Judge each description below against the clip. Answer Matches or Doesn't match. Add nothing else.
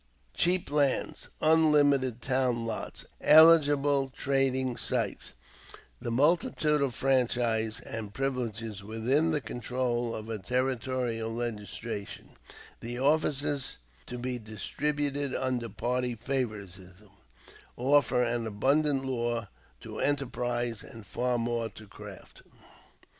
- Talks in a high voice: Doesn't match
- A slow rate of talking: Matches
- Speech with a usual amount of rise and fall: Matches